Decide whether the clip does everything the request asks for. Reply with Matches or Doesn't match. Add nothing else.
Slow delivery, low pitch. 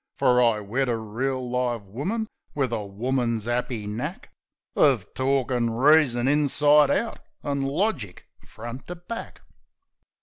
Matches